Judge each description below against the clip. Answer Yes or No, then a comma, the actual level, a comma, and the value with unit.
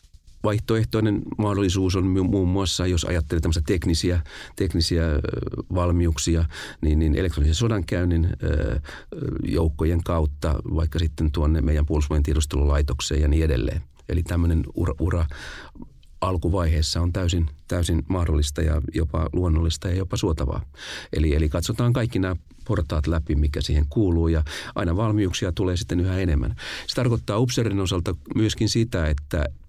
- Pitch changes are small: No, average, 3.1 semitones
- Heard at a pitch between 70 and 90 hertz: Yes, very low, 85 Hz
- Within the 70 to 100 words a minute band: No, average, 135 wpm